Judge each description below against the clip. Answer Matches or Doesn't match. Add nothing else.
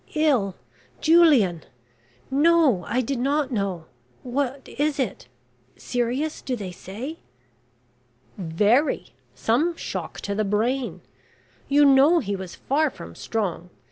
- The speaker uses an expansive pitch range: Matches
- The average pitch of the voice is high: Matches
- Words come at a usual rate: Doesn't match